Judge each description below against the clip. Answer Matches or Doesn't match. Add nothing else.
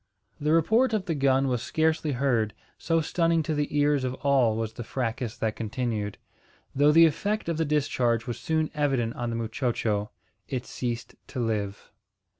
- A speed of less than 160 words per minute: Doesn't match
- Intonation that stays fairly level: Doesn't match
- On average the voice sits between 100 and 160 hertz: Matches